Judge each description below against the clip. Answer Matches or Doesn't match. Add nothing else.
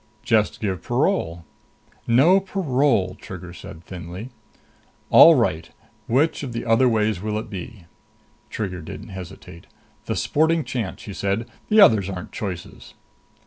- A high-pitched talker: Doesn't match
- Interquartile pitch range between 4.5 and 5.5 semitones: Matches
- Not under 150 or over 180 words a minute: Doesn't match